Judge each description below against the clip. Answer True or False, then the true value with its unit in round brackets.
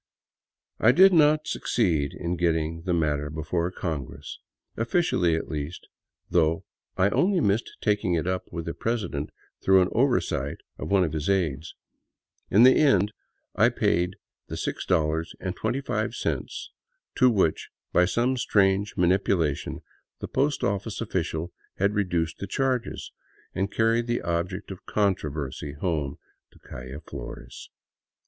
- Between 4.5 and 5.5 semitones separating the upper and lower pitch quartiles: True (5.2 semitones)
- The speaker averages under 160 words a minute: True (140 wpm)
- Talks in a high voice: False (90 Hz)